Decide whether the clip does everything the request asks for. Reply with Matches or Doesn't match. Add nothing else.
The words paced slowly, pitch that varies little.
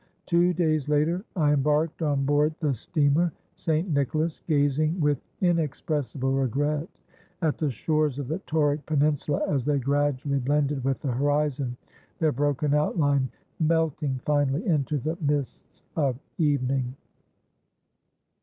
Matches